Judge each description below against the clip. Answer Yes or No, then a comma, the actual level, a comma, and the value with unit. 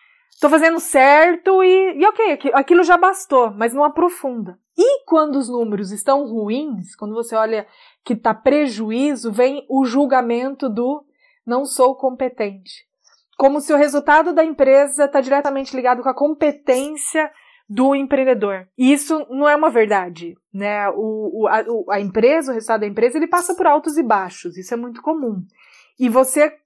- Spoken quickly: No, average, 165 wpm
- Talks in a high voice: Yes, very high, 270 Hz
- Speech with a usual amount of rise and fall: Yes, average, 4.8 semitones